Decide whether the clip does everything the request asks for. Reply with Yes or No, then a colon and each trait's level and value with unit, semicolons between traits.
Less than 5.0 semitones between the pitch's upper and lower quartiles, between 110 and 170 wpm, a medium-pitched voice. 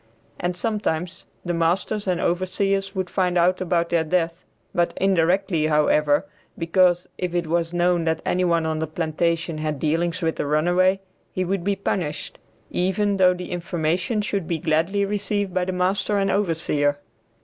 Yes: narrow, 2.4 semitones; average, 165 wpm; medium, 175 Hz